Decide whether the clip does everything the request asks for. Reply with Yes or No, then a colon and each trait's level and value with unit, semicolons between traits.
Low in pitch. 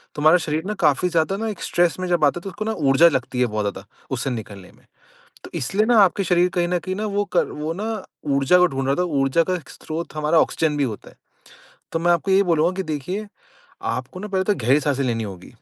No: medium, 165 Hz